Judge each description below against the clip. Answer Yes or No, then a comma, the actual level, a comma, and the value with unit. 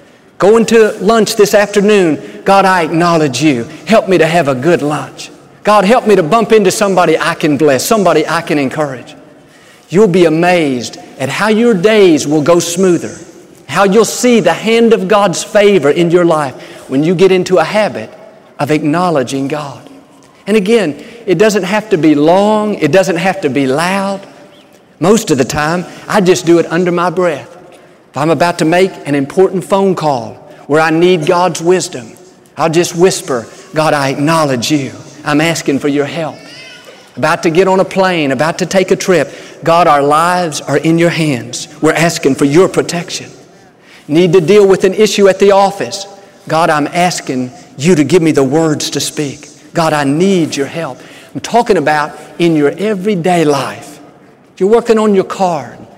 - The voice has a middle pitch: Yes, medium, 170 Hz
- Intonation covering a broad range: No, average, 4.3 semitones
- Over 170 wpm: Yes, average, 185 wpm